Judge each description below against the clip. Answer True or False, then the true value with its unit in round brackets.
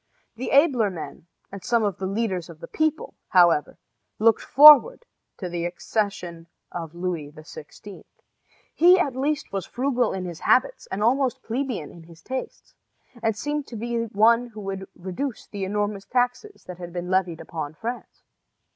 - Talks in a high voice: True (205 Hz)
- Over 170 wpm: False (165 wpm)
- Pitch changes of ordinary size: False (5.9 semitones)